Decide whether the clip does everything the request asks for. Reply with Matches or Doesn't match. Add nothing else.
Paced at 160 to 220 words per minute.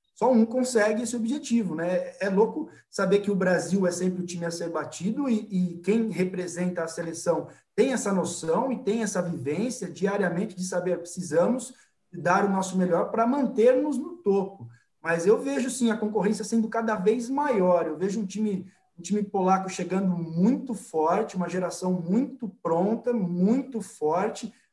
Matches